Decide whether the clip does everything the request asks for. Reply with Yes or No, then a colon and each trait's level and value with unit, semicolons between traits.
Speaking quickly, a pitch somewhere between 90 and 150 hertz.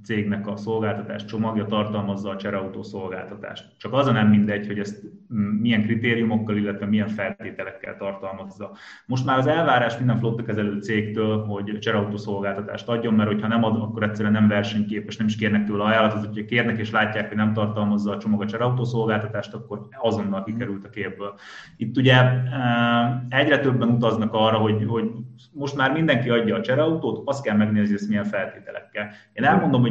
Yes: fast, 170 wpm; low, 110 Hz